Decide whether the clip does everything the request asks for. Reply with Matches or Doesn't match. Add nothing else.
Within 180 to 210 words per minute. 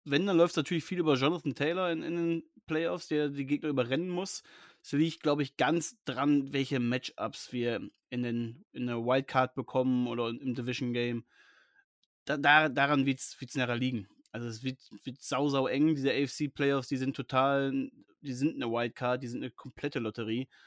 Matches